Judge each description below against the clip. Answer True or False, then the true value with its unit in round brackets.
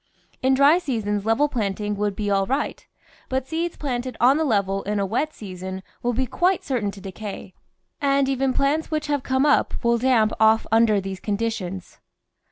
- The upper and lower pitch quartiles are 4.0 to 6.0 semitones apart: True (5.2 semitones)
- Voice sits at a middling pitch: False (230 Hz)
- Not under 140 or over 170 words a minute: False (180 wpm)